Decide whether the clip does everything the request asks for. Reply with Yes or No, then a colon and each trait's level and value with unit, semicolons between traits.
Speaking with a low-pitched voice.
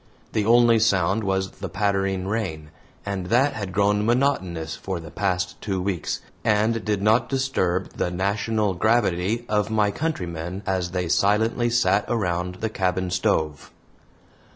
Yes: low, 100 Hz